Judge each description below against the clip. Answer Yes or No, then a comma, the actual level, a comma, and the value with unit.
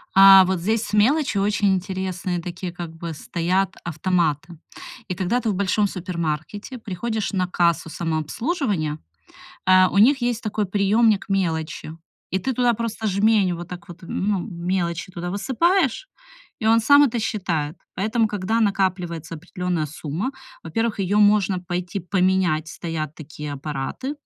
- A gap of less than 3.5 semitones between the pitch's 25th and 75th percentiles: No, average, 3.8 semitones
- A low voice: No, high, 190 Hz